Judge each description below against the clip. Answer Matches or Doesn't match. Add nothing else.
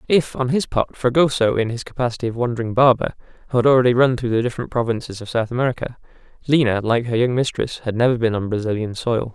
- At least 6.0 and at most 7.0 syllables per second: Matches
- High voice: Doesn't match